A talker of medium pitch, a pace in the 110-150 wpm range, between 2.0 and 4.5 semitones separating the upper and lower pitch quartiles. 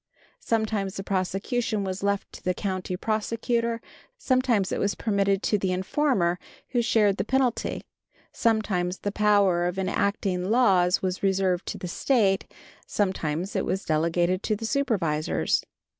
No: high, 195 Hz; average, 145 wpm; average, 3.2 semitones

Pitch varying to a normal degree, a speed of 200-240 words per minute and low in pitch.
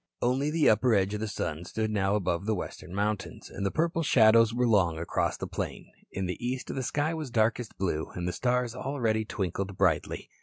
Yes: average, 4.4 semitones; fast, 205 wpm; low, 110 Hz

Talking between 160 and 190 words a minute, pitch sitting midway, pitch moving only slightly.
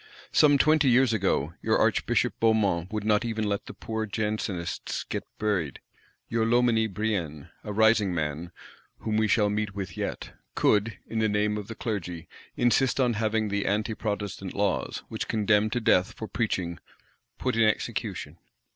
No: average, 165 wpm; low, 105 Hz; narrow, 2.3 semitones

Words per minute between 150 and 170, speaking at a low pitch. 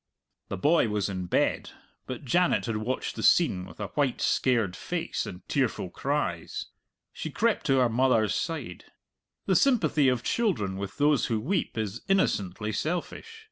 Yes: average, 160 wpm; low, 125 Hz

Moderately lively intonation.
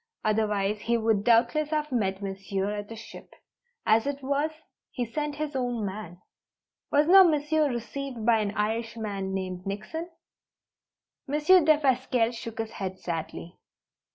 No: wide, 5.7 semitones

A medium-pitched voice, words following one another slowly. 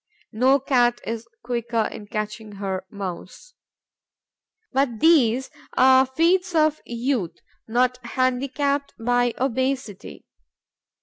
No: high, 245 Hz; slow, 105 wpm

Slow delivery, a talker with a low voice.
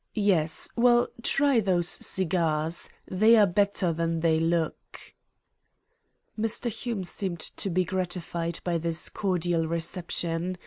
No: slow, 120 wpm; medium, 175 Hz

